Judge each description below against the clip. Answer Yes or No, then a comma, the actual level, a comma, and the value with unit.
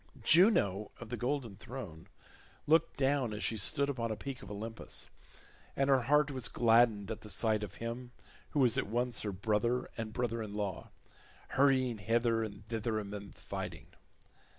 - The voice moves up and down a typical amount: Yes, average, 3.4 semitones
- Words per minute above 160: Yes, average, 175 wpm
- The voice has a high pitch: No, low, 115 Hz